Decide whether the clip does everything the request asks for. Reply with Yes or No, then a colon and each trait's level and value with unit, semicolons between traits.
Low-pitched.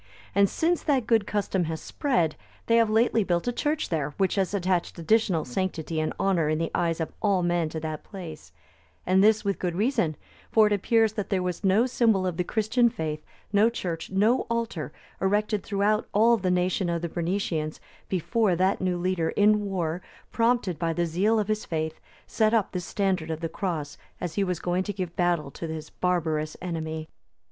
No: medium, 185 Hz